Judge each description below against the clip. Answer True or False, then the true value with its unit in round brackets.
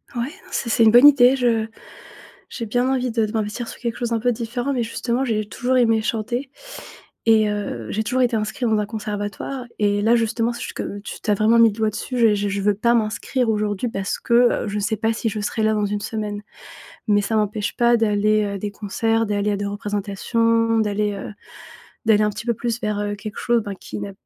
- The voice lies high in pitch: True (220 Hz)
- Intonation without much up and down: True (2.1 semitones)